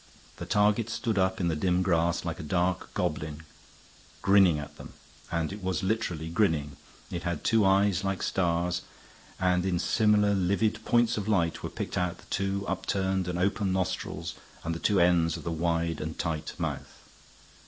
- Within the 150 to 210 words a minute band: Yes, average, 175 wpm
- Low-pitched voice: Yes, very low, 90 Hz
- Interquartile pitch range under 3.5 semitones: Yes, average, 2.9 semitones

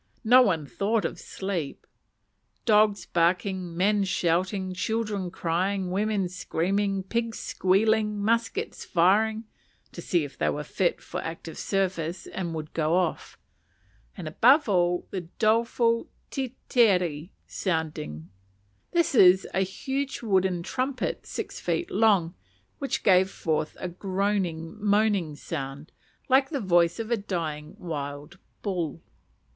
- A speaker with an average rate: No, slow, 125 wpm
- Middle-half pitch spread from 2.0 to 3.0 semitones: No, average, 4.2 semitones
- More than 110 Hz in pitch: Yes, high, 190 Hz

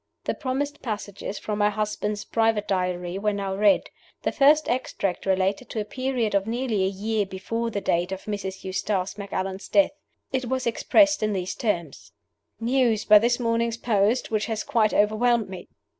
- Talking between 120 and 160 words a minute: No, average, 175 wpm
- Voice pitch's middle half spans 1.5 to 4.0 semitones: Yes, average, 3.3 semitones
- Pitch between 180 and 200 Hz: No, high, 210 Hz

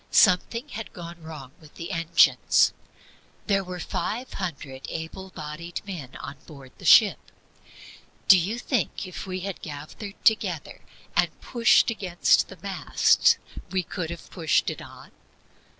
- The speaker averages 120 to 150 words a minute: Yes, average, 145 wpm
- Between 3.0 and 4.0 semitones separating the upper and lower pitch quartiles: Yes, average, 3.6 semitones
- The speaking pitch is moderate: Yes, medium, 180 Hz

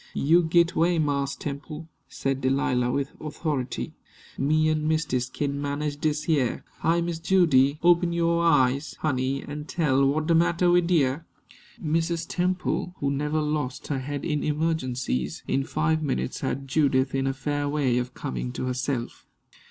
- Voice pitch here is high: No, medium, 150 Hz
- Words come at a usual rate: Yes, average, 160 wpm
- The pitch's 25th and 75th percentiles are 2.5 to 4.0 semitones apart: Yes, average, 3.2 semitones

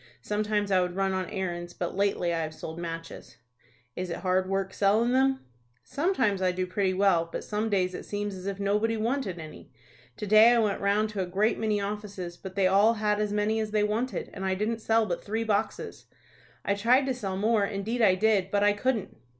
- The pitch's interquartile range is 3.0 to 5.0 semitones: No, narrow, 2.5 semitones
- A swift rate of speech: Yes, fast, 215 wpm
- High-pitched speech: Yes, high, 200 Hz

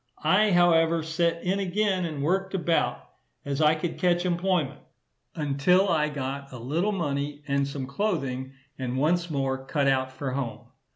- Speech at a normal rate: Yes, average, 160 wpm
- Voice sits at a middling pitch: Yes, medium, 155 Hz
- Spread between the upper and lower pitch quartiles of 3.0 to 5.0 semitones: Yes, average, 4.2 semitones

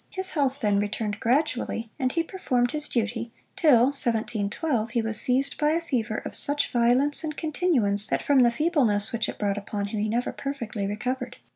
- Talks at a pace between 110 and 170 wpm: No, average, 185 wpm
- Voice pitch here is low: No, high, 245 Hz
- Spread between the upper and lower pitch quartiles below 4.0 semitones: No, average, 4.7 semitones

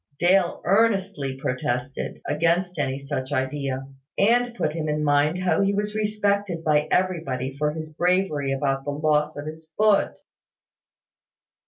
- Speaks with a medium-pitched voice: Yes, medium, 155 Hz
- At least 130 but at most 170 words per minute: Yes, average, 140 wpm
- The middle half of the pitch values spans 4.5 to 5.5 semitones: Yes, average, 5.1 semitones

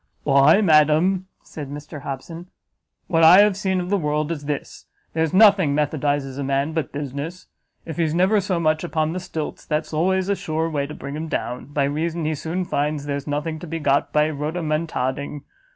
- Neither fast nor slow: Yes, average, 190 wpm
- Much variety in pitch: No, average, 2.8 semitones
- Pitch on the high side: No, medium, 155 Hz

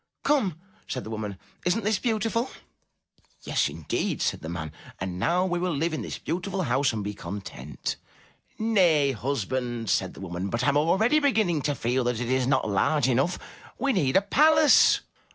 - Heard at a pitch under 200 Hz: Yes, medium, 140 Hz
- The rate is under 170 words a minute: No, average, 180 wpm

